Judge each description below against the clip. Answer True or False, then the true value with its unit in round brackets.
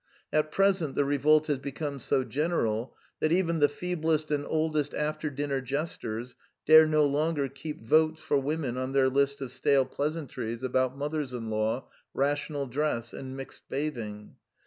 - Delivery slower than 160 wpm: False (165 wpm)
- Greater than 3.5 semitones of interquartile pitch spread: False (2.8 semitones)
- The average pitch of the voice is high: False (145 Hz)